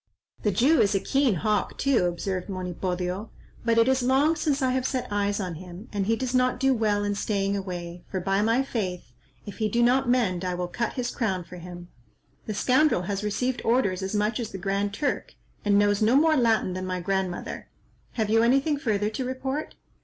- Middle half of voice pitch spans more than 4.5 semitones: Yes, average, 5.0 semitones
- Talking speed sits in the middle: No, fast, 210 wpm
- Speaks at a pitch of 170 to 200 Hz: No, high, 210 Hz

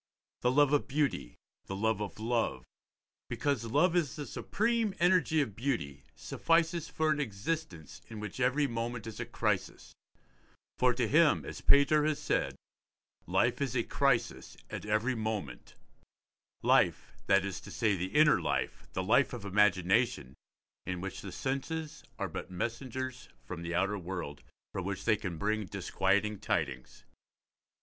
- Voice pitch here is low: Yes, low, 115 Hz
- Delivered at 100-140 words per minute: No, average, 155 wpm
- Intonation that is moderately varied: No, wide, 6.7 semitones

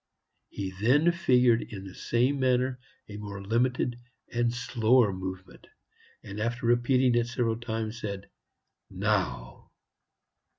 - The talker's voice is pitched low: Yes, low, 120 Hz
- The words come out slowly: Yes, slow, 120 wpm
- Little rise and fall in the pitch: No, average, 3.2 semitones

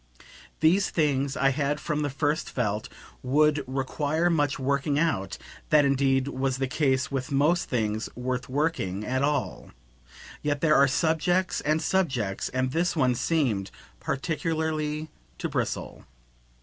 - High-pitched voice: No, medium, 140 Hz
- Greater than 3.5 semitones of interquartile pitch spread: No, average, 3.1 semitones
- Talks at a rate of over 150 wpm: No, slow, 135 wpm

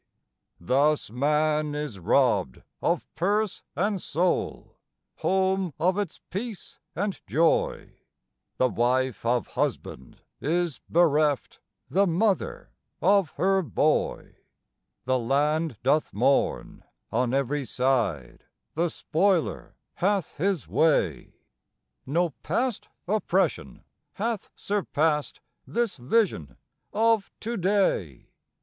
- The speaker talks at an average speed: No, slow, 100 wpm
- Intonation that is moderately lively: No, wide, 6.7 semitones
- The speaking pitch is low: No, medium, 160 Hz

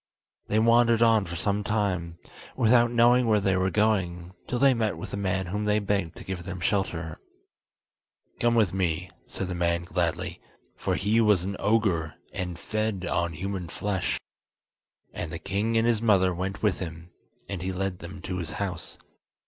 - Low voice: Yes, very low, 95 Hz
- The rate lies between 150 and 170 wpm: No, average, 180 wpm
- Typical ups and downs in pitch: Yes, average, 3.5 semitones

